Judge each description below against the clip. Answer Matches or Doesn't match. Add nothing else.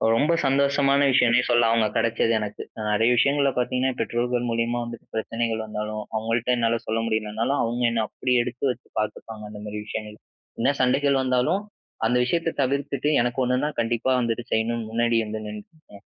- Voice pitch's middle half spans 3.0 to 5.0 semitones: Doesn't match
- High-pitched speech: Doesn't match